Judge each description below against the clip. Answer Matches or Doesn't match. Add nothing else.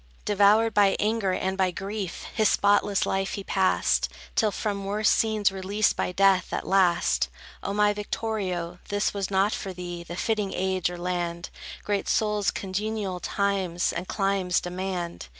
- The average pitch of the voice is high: Matches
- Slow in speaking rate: Doesn't match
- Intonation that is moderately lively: Doesn't match